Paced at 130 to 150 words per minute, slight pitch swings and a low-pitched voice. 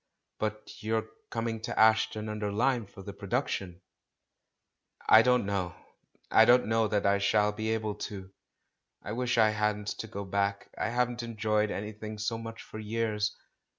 No: average, 165 wpm; narrow, 1.5 semitones; low, 110 Hz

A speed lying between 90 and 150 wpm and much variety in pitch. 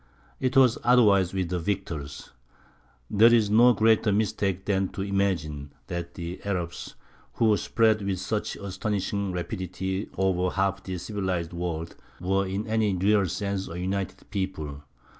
No: average, 140 wpm; narrow, 2.5 semitones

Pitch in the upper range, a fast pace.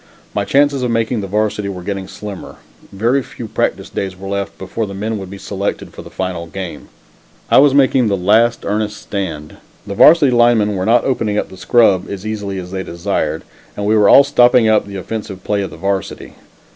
No: low, 105 Hz; fast, 215 wpm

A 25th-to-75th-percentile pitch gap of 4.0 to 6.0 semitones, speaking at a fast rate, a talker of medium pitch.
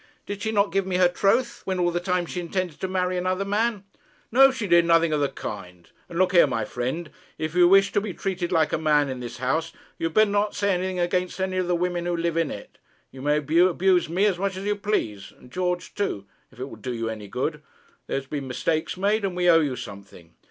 Yes: average, 4.3 semitones; fast, 250 wpm; medium, 175 Hz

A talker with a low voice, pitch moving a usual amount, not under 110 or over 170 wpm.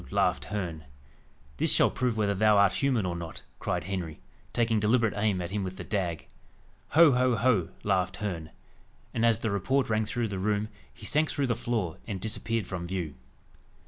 No: low, 105 Hz; average, 3.9 semitones; average, 185 wpm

